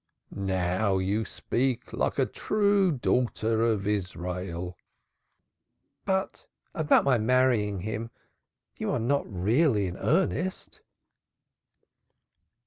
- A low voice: Yes, low, 110 Hz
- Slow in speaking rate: Yes, slow, 95 wpm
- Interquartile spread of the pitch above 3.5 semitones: Yes, wide, 5.6 semitones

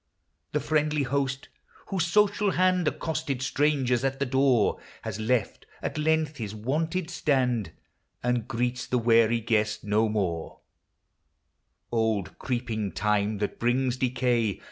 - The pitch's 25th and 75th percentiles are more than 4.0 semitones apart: Yes, average, 4.7 semitones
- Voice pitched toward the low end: Yes, low, 125 Hz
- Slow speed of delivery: Yes, slow, 125 wpm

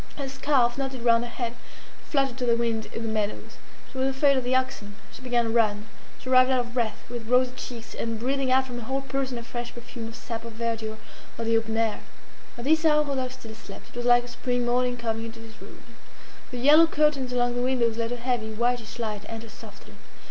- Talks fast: Yes, fast, 230 wpm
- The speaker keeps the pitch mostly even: Yes, narrow, 2.2 semitones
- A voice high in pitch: Yes, high, 240 Hz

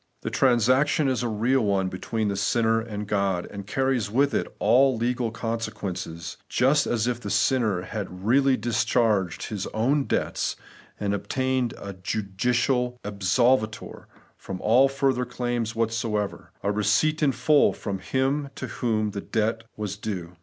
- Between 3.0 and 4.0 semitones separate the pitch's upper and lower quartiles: Yes, average, 3.6 semitones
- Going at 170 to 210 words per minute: No, average, 155 wpm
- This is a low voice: Yes, low, 115 Hz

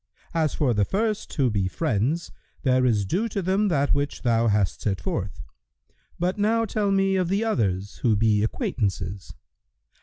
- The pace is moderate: Yes, average, 175 wpm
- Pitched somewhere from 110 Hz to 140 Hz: Yes, low, 135 Hz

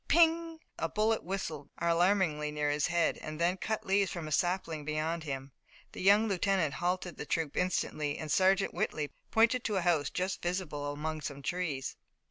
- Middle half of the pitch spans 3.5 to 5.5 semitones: Yes, average, 4.2 semitones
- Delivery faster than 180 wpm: No, average, 175 wpm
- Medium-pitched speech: Yes, medium, 170 Hz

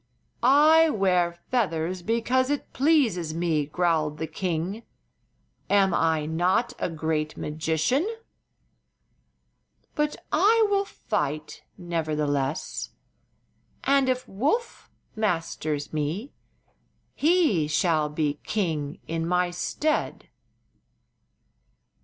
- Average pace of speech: No, slow, 90 wpm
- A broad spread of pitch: Yes, wide, 8.3 semitones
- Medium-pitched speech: Yes, medium, 175 Hz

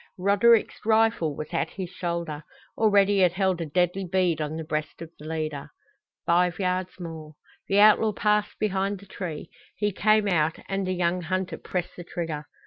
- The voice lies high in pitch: No, medium, 180 Hz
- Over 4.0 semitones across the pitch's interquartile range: No, average, 3.4 semitones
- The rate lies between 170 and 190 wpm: Yes, average, 175 wpm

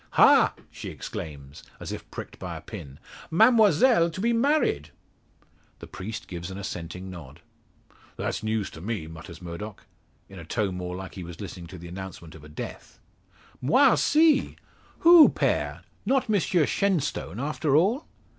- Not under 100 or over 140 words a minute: No, average, 155 wpm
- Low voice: Yes, low, 100 Hz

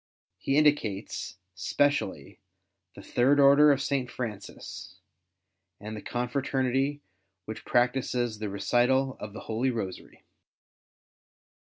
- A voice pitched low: Yes, low, 125 Hz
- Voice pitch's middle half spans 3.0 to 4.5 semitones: Yes, average, 4.0 semitones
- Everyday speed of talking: No, slow, 105 wpm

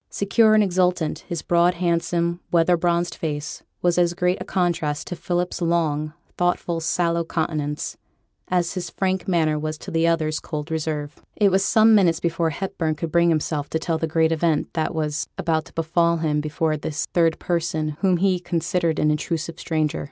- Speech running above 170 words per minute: Yes, average, 180 wpm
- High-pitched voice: No, medium, 170 Hz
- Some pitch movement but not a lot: No, narrow, 2.0 semitones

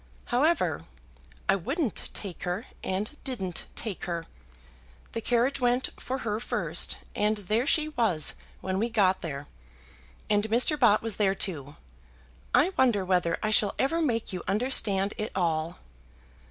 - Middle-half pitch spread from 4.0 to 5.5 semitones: Yes, average, 4.7 semitones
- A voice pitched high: Yes, high, 210 Hz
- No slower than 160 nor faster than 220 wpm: No, average, 145 wpm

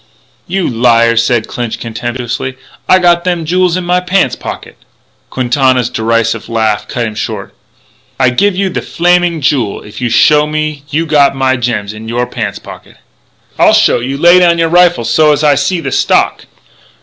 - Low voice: Yes, low, 130 Hz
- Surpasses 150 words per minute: Yes, average, 175 wpm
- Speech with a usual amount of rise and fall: No, wide, 6.6 semitones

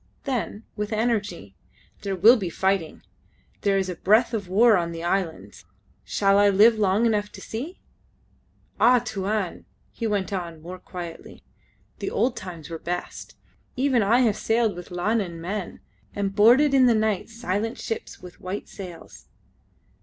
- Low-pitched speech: No, high, 205 Hz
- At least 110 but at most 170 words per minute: Yes, average, 155 wpm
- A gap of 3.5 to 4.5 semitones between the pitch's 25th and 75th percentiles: Yes, average, 3.8 semitones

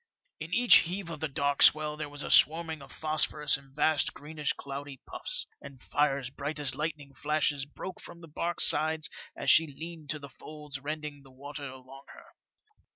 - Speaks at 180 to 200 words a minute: Yes, average, 185 wpm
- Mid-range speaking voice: Yes, medium, 150 Hz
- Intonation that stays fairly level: Yes, narrow, 2.0 semitones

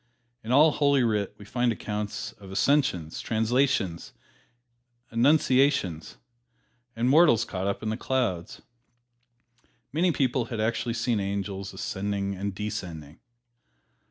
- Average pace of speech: No, slow, 115 wpm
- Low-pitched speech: Yes, low, 110 Hz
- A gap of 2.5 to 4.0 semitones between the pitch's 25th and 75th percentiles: No, average, 4.7 semitones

